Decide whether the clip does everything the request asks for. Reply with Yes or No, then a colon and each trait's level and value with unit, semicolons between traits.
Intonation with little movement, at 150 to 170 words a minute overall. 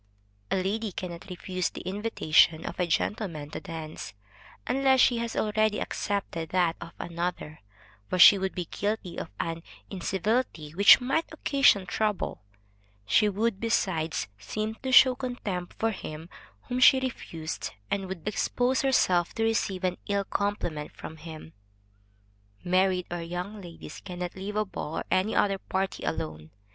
No: average, 4.3 semitones; average, 155 wpm